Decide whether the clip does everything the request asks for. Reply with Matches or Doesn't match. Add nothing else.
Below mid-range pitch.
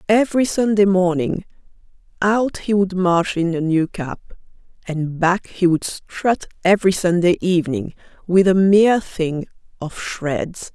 Doesn't match